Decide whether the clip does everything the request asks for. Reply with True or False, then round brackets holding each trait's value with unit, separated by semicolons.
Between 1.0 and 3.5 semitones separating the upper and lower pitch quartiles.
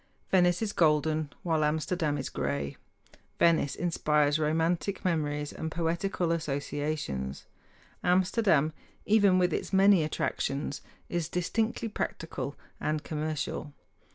True (3.1 semitones)